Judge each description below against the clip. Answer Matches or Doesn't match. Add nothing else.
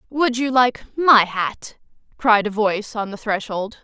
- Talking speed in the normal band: Matches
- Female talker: Matches